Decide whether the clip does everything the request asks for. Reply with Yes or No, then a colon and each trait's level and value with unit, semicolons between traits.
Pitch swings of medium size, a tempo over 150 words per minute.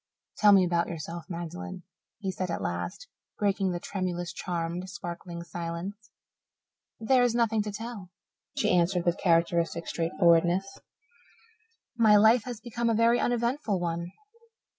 No: average, 4.0 semitones; slow, 135 wpm